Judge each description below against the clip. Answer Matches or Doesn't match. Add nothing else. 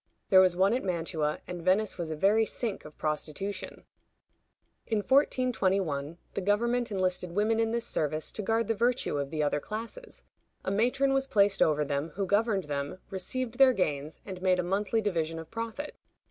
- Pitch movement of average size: Doesn't match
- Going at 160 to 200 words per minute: Matches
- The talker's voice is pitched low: Doesn't match